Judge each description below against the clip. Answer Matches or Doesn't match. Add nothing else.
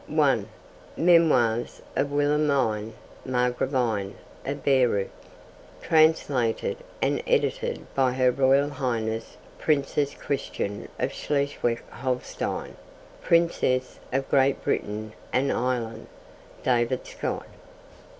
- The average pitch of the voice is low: Matches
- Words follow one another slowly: Matches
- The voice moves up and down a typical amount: Matches